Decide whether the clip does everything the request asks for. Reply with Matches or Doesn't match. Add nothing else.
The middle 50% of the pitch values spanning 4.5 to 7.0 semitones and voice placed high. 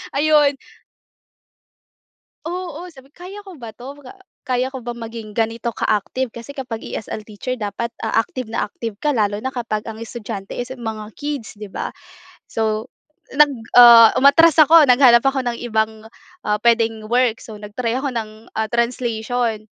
Doesn't match